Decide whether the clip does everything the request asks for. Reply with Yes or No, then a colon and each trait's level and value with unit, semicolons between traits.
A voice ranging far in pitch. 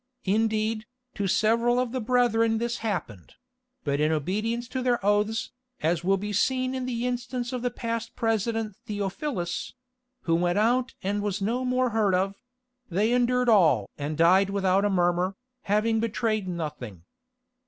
No: average, 4.4 semitones